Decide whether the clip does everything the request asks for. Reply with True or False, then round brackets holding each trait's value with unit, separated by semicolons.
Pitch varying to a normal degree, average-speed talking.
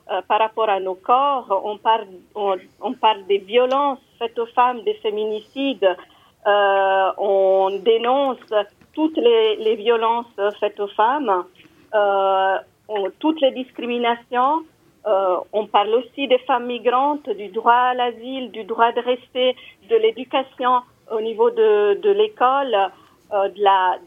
False (4.8 semitones; 140 wpm)